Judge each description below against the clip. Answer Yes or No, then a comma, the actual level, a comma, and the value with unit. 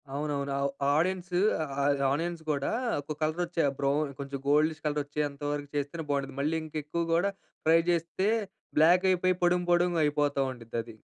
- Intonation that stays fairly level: No, average, 3.1 semitones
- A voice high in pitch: No, medium, 150 Hz